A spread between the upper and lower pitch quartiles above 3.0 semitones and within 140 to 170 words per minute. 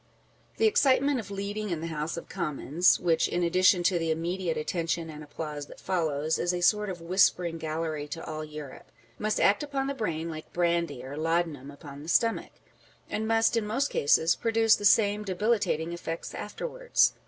No: average, 4.8 semitones; average, 180 wpm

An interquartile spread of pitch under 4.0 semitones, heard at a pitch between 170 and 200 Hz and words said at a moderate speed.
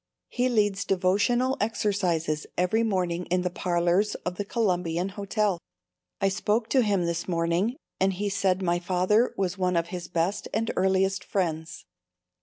Yes: average, 2.9 semitones; high, 190 Hz; average, 155 wpm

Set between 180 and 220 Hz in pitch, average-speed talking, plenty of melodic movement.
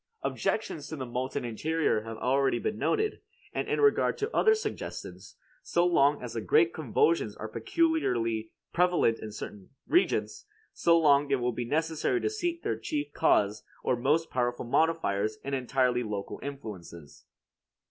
No: low, 135 Hz; average, 155 wpm; wide, 6.2 semitones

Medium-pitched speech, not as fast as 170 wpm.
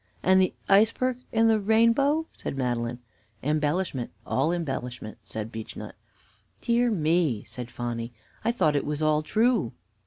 Yes: medium, 155 Hz; slow, 135 wpm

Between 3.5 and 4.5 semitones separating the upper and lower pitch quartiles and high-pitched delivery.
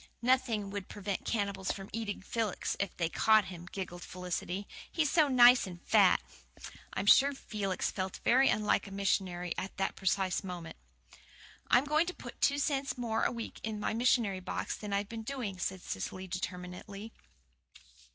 Yes: average, 4.0 semitones; high, 200 Hz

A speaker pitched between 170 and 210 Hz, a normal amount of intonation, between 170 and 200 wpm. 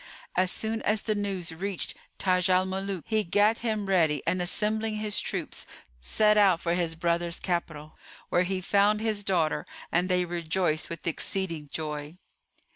No: medium, 185 Hz; average, 3.4 semitones; average, 160 wpm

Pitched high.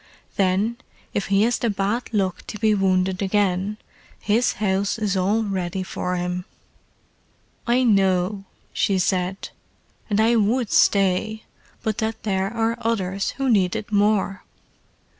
Yes: high, 200 Hz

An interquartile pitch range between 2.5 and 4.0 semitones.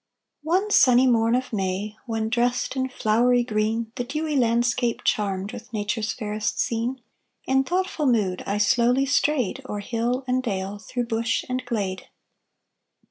Yes: average, 3.2 semitones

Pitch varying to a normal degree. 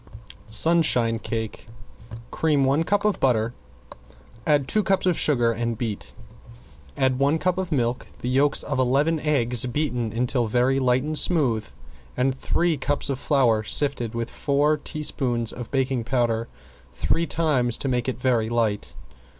Yes: average, 4.0 semitones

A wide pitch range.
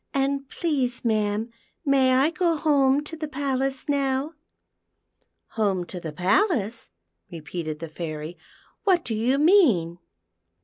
Yes: wide, 8.1 semitones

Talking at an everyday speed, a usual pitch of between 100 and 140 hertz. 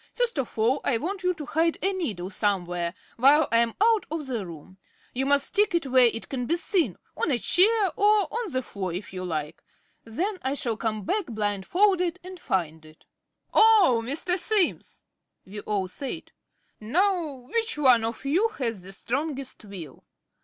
No: average, 180 wpm; very high, 265 Hz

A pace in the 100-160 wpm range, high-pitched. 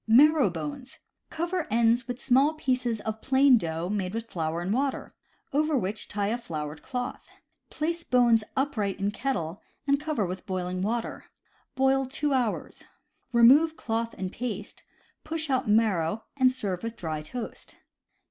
Yes: average, 155 wpm; high, 230 Hz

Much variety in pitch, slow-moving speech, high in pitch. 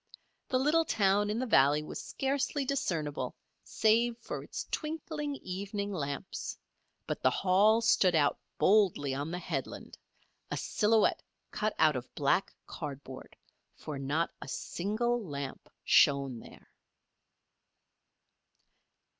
Yes: wide, 8.0 semitones; slow, 120 wpm; high, 195 Hz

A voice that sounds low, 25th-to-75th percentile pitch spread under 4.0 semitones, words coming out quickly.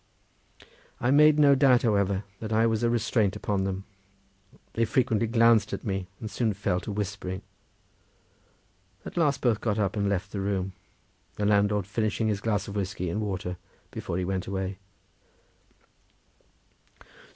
No: low, 105 Hz; average, 2.8 semitones; average, 150 wpm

